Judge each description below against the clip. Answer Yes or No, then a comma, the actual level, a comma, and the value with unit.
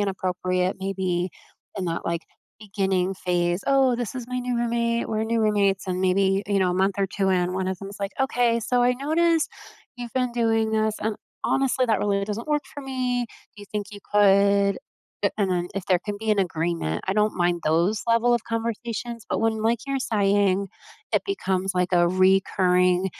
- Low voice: No, high, 200 Hz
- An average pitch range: Yes, average, 3.9 semitones